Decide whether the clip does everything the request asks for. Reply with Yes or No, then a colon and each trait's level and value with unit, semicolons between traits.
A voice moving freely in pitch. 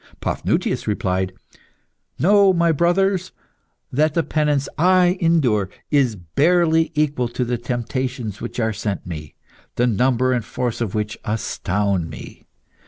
Yes: wide, 7.3 semitones